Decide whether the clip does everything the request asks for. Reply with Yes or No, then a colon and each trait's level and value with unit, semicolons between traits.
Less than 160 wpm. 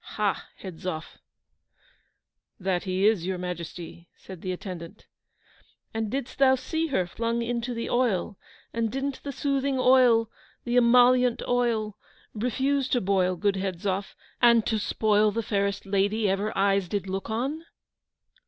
Yes: average, 140 wpm